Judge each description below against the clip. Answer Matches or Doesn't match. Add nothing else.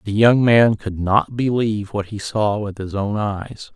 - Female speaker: Doesn't match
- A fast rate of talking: Matches